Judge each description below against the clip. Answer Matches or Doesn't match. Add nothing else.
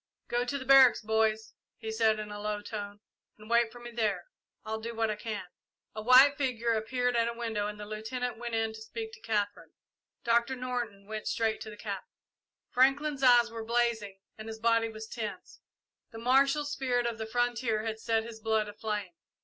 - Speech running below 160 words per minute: Doesn't match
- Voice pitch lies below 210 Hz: Doesn't match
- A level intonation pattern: Matches